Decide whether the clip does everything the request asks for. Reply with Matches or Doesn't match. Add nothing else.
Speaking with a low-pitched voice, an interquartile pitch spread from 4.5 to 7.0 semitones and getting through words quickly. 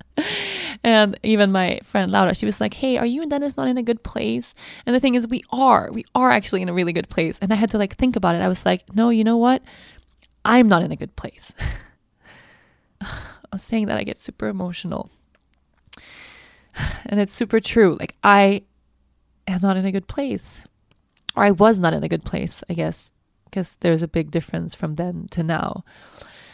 Doesn't match